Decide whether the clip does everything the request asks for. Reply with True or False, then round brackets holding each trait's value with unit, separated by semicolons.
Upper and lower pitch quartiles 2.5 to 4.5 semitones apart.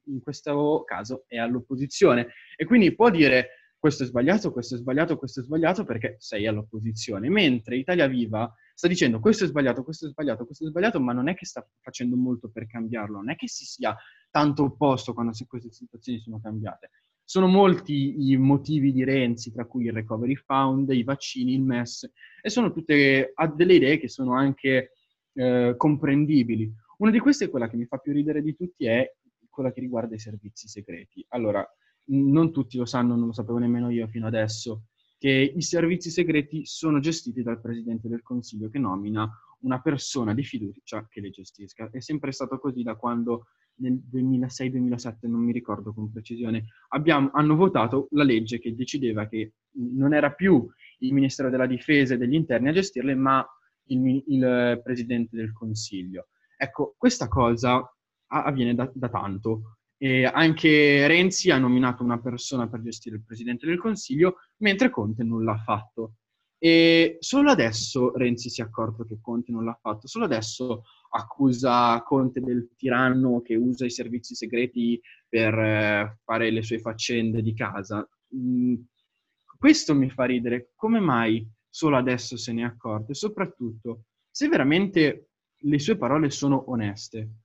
True (3.9 semitones)